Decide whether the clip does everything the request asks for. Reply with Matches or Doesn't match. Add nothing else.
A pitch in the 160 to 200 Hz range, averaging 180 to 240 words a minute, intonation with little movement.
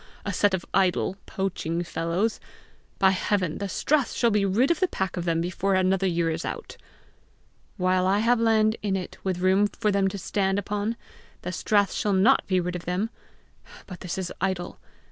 Matches